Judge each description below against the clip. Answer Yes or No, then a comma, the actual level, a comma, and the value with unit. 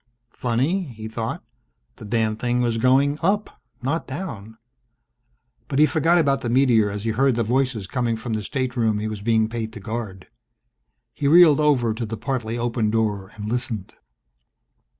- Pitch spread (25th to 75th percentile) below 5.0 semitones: Yes, average, 3.6 semitones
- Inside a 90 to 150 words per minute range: No, average, 170 wpm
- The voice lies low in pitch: Yes, low, 120 Hz